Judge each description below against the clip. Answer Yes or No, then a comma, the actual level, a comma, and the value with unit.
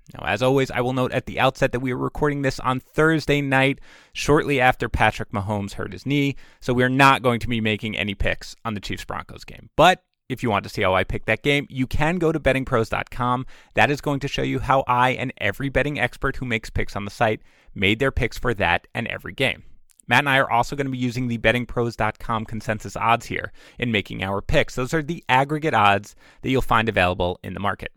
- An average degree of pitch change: Yes, average, 3.8 semitones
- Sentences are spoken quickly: Yes, fast, 240 wpm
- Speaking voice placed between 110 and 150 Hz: Yes, low, 125 Hz